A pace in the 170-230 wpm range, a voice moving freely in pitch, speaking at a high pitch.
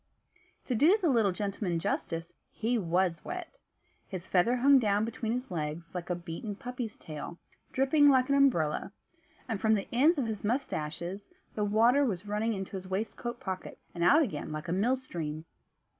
Yes: average, 175 wpm; wide, 6.2 semitones; high, 210 Hz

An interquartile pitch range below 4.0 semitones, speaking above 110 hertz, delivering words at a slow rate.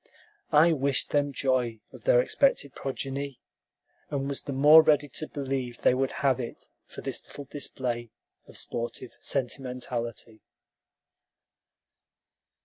Yes: narrow, 2.4 semitones; low, 135 Hz; slow, 125 wpm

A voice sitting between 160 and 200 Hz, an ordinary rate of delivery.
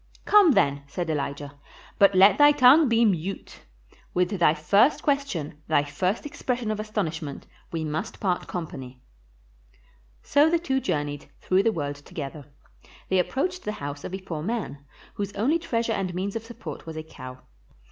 Yes: medium, 185 Hz; average, 165 wpm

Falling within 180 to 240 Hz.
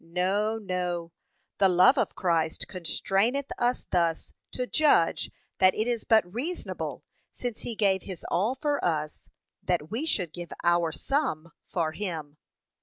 Yes: medium, 185 Hz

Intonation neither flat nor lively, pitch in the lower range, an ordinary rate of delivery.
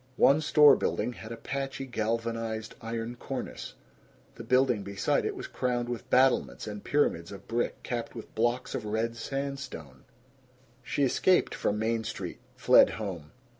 Yes: average, 3.0 semitones; low, 115 Hz; average, 150 wpm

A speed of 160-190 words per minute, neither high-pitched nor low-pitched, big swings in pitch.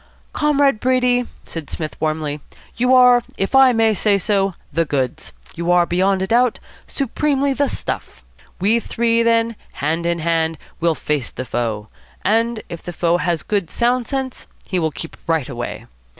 No: average, 165 wpm; high, 195 Hz; wide, 6.9 semitones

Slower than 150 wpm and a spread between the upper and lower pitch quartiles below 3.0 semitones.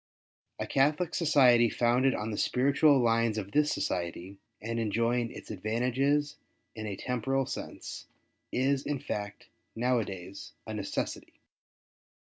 No: slow, 135 wpm; average, 3.9 semitones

